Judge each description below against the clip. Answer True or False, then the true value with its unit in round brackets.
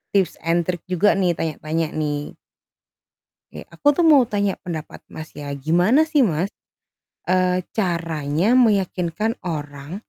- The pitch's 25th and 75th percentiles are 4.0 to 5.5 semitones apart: True (4.4 semitones)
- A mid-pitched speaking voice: True (175 Hz)